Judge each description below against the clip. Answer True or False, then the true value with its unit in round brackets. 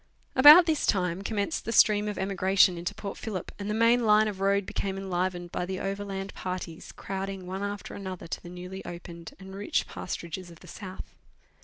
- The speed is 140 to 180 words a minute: False (190 wpm)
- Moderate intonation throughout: False (2.0 semitones)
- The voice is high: True (195 Hz)